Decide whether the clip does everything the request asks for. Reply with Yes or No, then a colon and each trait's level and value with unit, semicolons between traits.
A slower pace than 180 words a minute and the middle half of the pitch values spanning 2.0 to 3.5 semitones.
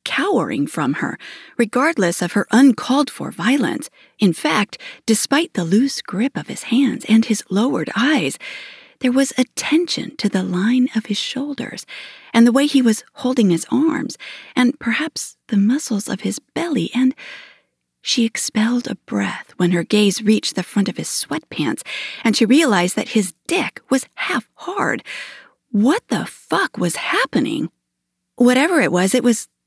No: average, 160 wpm; average, 4.8 semitones